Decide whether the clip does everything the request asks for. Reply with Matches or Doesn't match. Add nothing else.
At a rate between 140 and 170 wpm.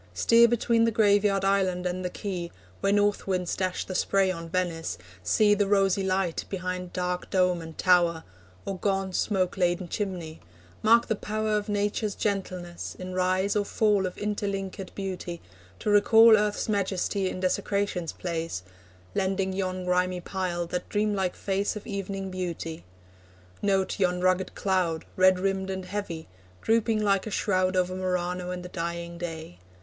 Matches